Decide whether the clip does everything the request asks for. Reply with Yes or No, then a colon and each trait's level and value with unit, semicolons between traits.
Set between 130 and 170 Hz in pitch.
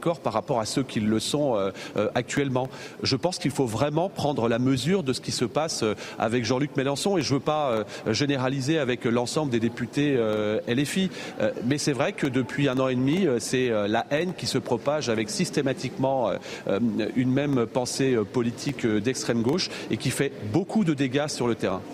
Yes: low, 135 Hz